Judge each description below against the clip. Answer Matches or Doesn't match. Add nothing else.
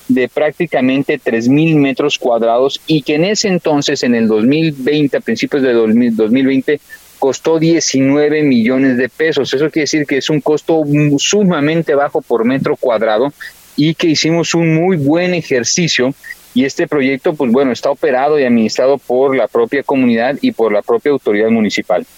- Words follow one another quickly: Doesn't match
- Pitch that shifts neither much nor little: Matches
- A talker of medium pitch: Matches